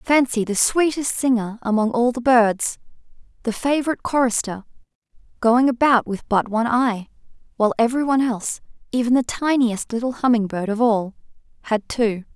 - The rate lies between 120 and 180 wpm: Yes, average, 150 wpm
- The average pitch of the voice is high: Yes, high, 235 Hz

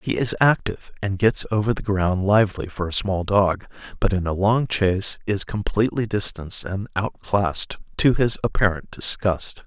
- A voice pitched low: Yes, low, 100 Hz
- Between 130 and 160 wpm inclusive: No, average, 170 wpm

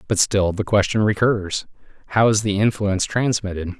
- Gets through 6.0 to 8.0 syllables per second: No, 5.2 syllables/s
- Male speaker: Yes, male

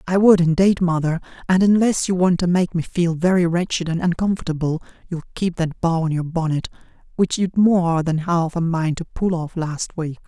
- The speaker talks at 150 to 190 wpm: No, fast, 205 wpm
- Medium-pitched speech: Yes, medium, 170 Hz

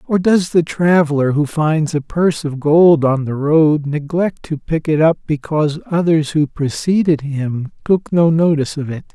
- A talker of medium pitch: Yes, medium, 155 Hz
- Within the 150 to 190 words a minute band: Yes, average, 185 wpm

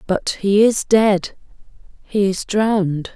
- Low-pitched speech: No, high, 200 Hz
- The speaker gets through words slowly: Yes, slow, 115 wpm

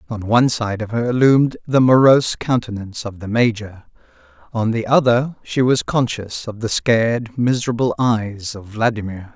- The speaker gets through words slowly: No, average, 160 wpm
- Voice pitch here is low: Yes, low, 115 Hz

